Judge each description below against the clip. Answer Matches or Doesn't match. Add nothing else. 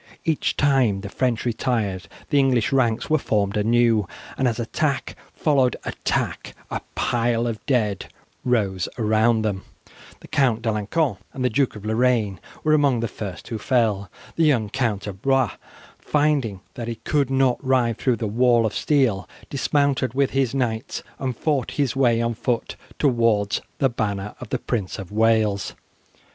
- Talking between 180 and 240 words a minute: Doesn't match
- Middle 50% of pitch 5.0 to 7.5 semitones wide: Doesn't match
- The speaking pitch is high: Doesn't match